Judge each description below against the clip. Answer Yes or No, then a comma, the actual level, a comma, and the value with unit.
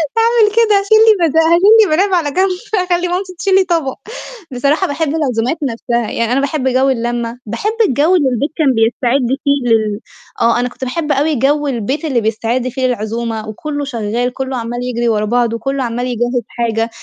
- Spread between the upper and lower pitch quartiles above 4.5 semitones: Yes, average, 5.3 semitones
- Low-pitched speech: No, very high, 260 Hz